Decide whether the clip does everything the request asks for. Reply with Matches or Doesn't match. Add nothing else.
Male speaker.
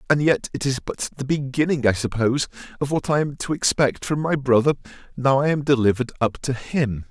Matches